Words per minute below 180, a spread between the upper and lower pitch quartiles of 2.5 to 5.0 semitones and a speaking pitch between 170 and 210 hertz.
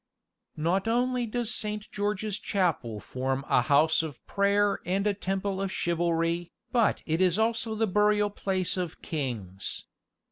Yes: average, 145 wpm; average, 4.4 semitones; high, 190 Hz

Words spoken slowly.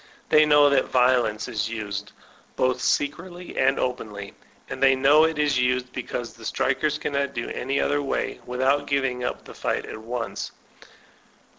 No: average, 165 wpm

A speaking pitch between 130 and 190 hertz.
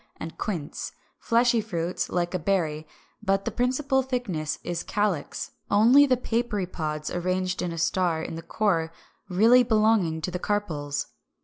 Yes: medium, 185 Hz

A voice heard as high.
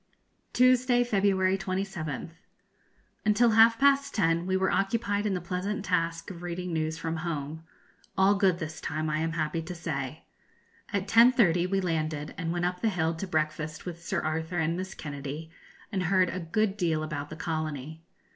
No: medium, 175 Hz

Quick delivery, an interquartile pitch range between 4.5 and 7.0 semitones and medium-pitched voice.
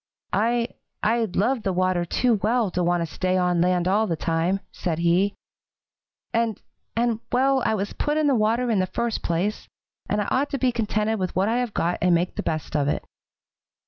No: fast, 210 wpm; average, 4.8 semitones; high, 205 Hz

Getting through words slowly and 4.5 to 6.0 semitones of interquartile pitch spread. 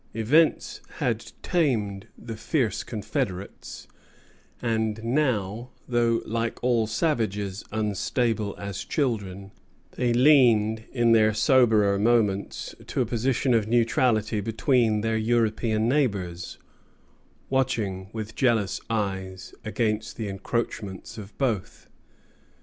No: slow, 105 wpm; average, 2.7 semitones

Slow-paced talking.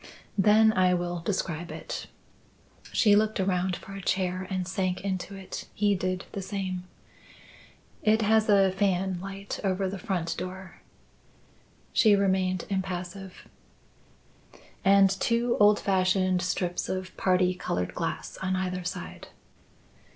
Yes: slow, 125 wpm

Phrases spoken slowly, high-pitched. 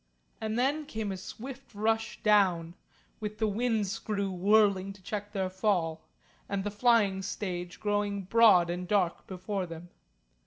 No: average, 150 wpm; high, 205 Hz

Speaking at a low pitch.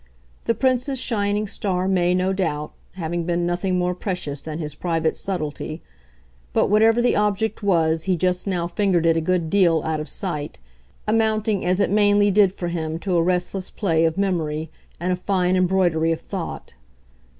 No: medium, 180 Hz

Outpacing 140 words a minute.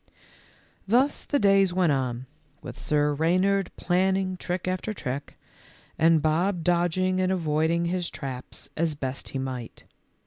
No: slow, 135 wpm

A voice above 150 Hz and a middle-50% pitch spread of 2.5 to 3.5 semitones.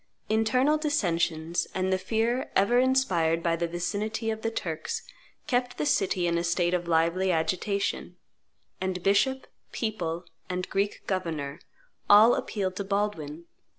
No: high, 190 Hz; average, 4.3 semitones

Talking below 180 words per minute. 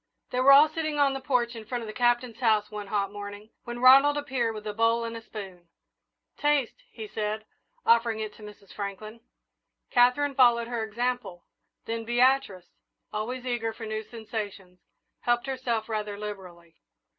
Yes: average, 170 wpm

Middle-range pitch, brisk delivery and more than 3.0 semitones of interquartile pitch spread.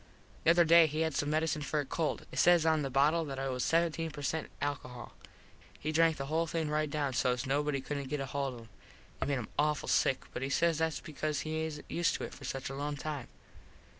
No: medium, 150 Hz; fast, 240 wpm; narrow, 2.6 semitones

